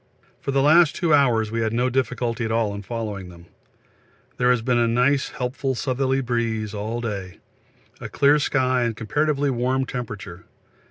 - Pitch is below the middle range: Yes, low, 120 Hz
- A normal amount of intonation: Yes, average, 3.1 semitones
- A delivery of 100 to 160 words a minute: No, average, 170 wpm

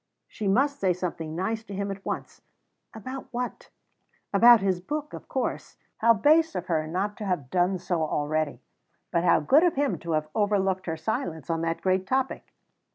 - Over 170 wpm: Yes, average, 185 wpm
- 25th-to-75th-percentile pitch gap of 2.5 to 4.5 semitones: No, average, 5.1 semitones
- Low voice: No, high, 190 Hz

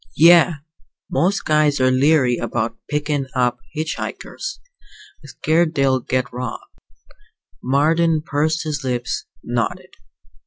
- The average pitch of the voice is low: No, medium, 145 Hz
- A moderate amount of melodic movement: Yes, average, 3.8 semitones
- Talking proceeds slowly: Yes, slow, 110 wpm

